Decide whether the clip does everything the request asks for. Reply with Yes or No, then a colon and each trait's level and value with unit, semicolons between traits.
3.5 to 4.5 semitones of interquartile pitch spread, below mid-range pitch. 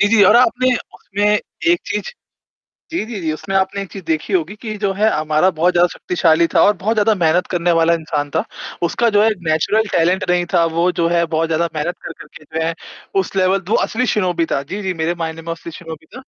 No: average, 3.9 semitones; medium, 180 Hz